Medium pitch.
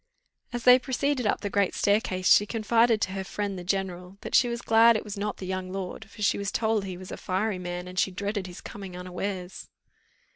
No: high, 200 Hz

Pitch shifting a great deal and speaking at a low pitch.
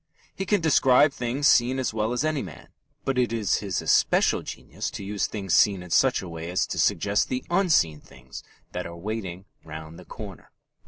Yes: wide, 6.7 semitones; low, 110 Hz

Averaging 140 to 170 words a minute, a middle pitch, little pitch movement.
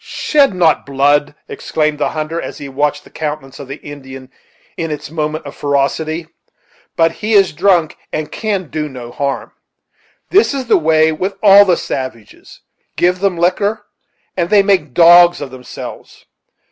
No: average, 160 wpm; medium, 155 Hz; average, 4.2 semitones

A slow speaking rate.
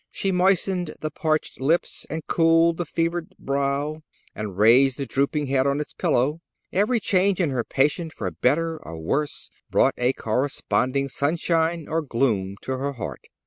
No: average, 160 wpm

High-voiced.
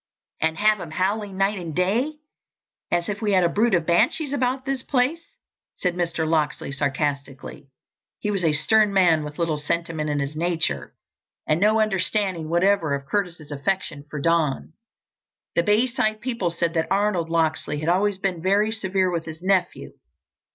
No: medium, 180 Hz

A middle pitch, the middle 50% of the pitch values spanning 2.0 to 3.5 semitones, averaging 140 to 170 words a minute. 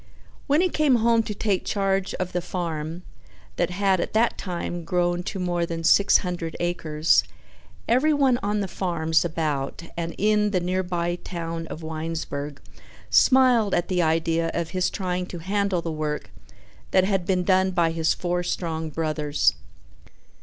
Yes: medium, 175 Hz; average, 2.9 semitones; average, 160 wpm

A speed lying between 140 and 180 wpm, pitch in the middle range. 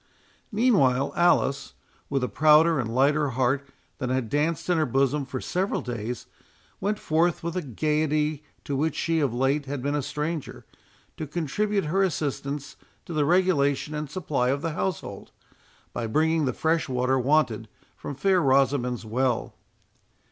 Yes: average, 160 wpm; medium, 145 Hz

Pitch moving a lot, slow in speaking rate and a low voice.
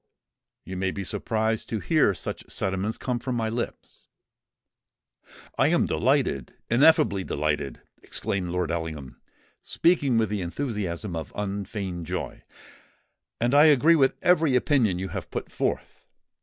Yes: wide, 5.8 semitones; slow, 130 wpm; low, 105 Hz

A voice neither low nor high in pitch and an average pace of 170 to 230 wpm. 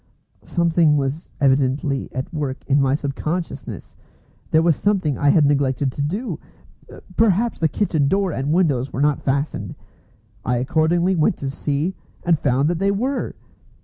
No: medium, 150 Hz; average, 155 wpm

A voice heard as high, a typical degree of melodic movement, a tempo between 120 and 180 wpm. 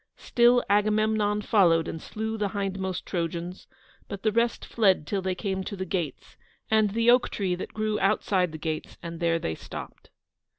Yes: high, 195 Hz; average, 3.4 semitones; average, 175 wpm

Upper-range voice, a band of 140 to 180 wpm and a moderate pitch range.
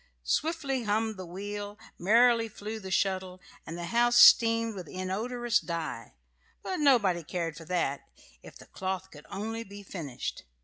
Yes: high, 205 Hz; average, 150 wpm; average, 4.1 semitones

